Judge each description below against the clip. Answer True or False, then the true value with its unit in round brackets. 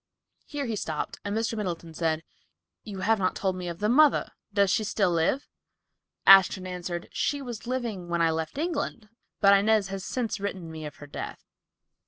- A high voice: True (195 Hz)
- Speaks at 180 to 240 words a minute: True (185 wpm)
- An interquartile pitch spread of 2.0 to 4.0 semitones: False (4.4 semitones)